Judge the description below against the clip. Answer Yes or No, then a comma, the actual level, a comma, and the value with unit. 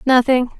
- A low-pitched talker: No, very high, 250 Hz